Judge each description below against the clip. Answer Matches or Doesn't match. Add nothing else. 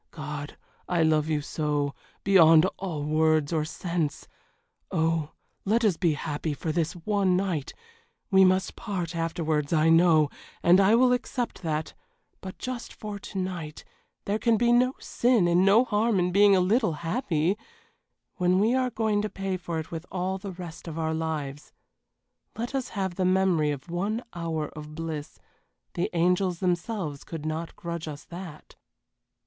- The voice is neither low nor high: Matches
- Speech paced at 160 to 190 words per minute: Matches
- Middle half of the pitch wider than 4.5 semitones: Doesn't match